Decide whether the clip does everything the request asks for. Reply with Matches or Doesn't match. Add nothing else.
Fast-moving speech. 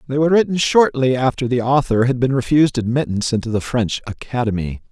Doesn't match